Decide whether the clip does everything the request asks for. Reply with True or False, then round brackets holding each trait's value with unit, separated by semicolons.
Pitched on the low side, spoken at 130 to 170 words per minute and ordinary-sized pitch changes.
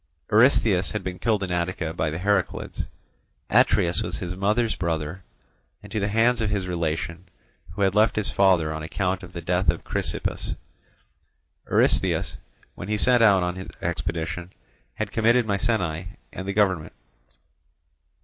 True (95 Hz; 155 wpm; 3.4 semitones)